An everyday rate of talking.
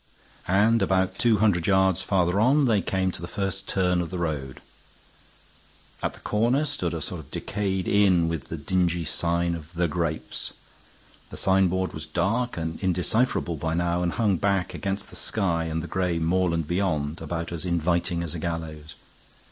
Yes: average, 175 wpm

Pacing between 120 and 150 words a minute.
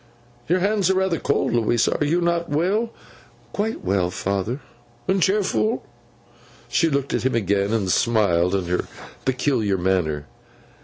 Yes: average, 145 wpm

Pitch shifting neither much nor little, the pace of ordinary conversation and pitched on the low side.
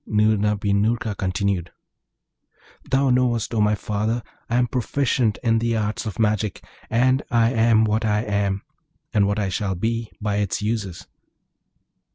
No: narrow, 2.2 semitones; average, 155 wpm; low, 110 Hz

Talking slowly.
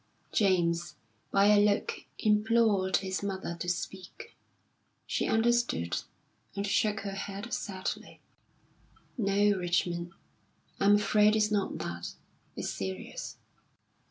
Yes: slow, 105 wpm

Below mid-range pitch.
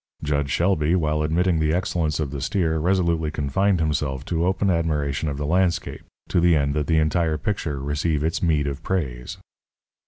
Yes: very low, 80 Hz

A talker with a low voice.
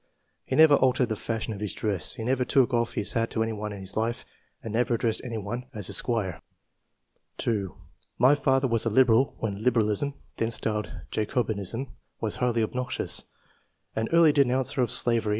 Yes: low, 115 Hz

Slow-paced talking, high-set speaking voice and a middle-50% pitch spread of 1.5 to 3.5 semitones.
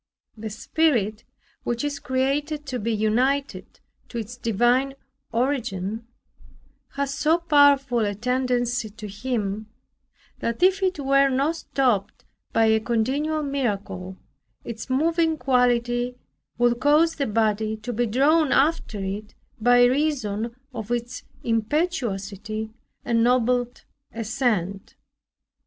No: slow, 115 wpm; high, 245 Hz; average, 4.1 semitones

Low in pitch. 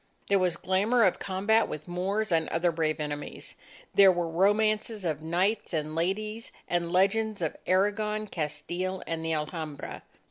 No: medium, 185 Hz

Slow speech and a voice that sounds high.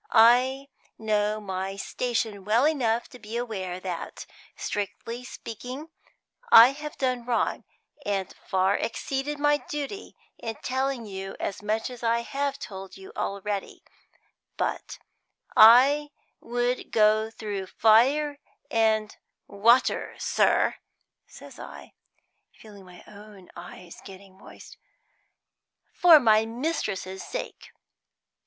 Yes: slow, 110 wpm; high, 225 Hz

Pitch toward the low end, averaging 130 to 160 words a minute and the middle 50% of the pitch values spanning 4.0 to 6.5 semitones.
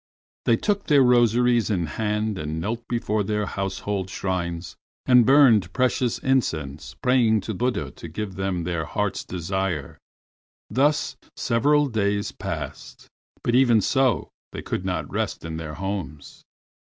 Yes: low, 105 Hz; average, 140 wpm; wide, 5.4 semitones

